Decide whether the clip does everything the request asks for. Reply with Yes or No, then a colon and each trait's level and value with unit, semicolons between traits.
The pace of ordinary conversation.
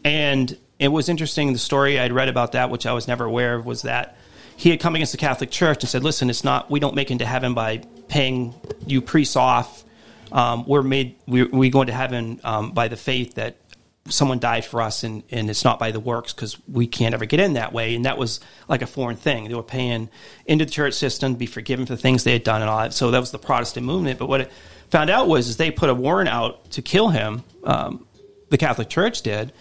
No: fast, 255 wpm